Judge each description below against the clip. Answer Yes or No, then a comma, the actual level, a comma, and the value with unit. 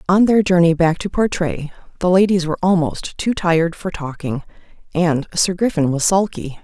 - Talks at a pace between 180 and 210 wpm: No, average, 170 wpm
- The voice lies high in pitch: No, medium, 175 Hz